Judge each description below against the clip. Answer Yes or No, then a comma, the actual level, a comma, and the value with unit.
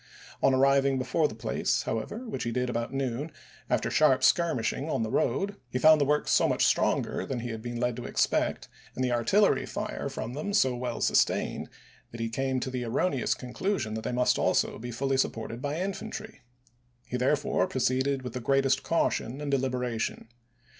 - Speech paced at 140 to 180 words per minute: No, average, 190 wpm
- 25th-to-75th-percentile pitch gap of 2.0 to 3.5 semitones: Yes, average, 3.0 semitones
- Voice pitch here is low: Yes, low, 130 Hz